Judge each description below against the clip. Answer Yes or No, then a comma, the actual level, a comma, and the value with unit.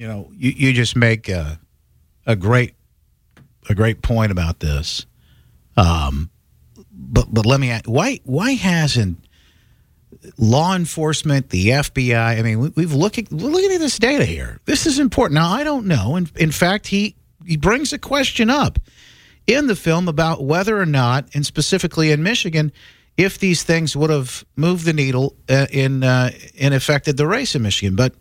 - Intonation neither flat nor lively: No, wide, 7.2 semitones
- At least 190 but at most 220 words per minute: No, average, 180 wpm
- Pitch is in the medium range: Yes, medium, 145 Hz